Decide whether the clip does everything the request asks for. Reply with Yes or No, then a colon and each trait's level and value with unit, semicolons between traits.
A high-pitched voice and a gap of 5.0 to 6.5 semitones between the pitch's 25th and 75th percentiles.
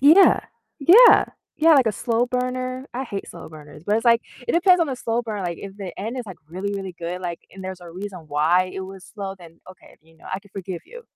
Yes: high, 200 Hz; wide, 5.6 semitones